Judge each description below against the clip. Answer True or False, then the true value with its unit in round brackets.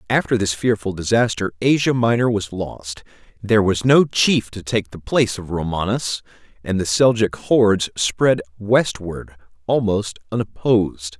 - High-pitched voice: False (105 Hz)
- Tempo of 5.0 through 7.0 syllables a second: False (4.6 syllables/s)